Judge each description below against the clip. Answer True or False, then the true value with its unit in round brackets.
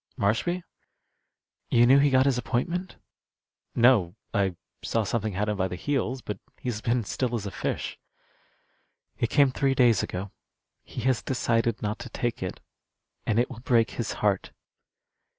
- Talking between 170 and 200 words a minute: False (160 wpm)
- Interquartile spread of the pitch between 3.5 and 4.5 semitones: True (3.8 semitones)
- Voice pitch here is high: False (115 Hz)